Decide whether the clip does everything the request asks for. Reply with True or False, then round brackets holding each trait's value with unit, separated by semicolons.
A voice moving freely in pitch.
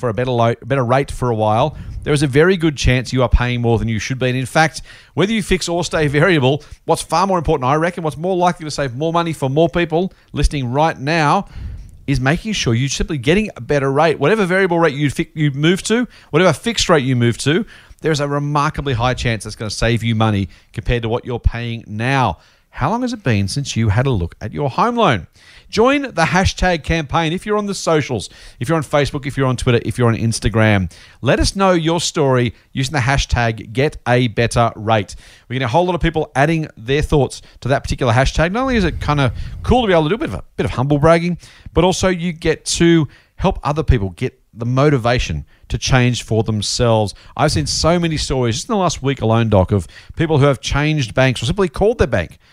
True (5.9 semitones)